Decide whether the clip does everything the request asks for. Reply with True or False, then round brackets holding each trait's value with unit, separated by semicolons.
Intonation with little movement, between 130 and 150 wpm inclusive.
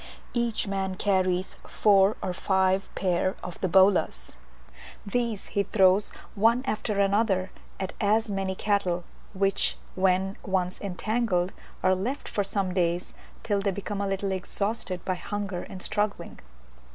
True (1.7 semitones; 140 wpm)